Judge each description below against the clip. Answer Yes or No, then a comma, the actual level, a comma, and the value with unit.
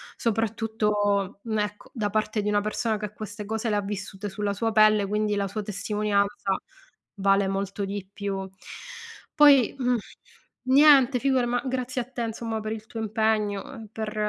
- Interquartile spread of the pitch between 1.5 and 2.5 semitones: Yes, narrow, 1.9 semitones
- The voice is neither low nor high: No, high, 215 Hz